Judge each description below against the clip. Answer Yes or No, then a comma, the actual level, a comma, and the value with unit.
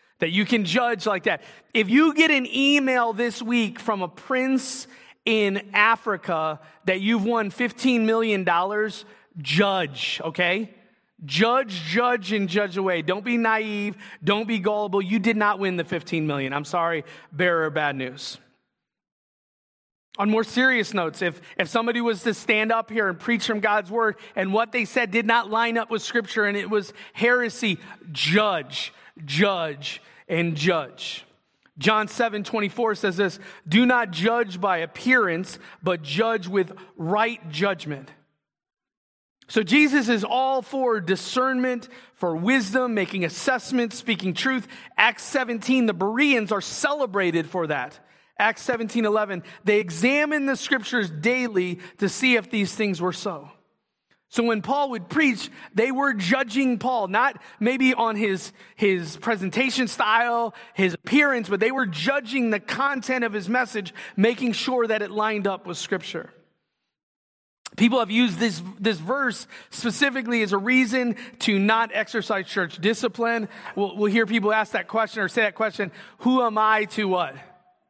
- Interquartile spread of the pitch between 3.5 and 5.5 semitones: Yes, average, 4.0 semitones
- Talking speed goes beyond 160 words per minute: No, average, 155 wpm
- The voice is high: Yes, high, 215 Hz